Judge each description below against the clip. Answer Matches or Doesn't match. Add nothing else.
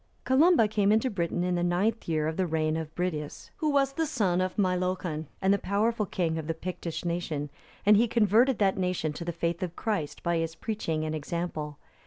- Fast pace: Matches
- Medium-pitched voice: Matches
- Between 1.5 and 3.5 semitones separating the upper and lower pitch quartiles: Doesn't match